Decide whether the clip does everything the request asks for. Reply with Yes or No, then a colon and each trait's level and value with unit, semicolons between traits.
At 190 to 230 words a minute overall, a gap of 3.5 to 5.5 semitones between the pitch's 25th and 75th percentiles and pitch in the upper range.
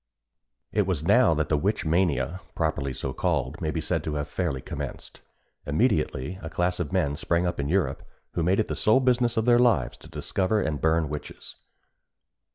No: average, 195 wpm; average, 4.7 semitones; very low, 85 Hz